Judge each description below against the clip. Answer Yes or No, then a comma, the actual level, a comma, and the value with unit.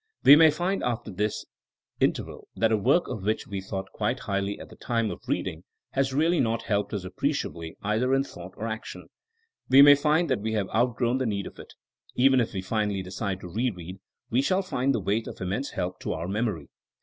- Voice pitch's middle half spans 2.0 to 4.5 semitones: No, average, 5.1 semitones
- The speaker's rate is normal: No, fast, 225 wpm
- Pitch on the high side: No, low, 110 Hz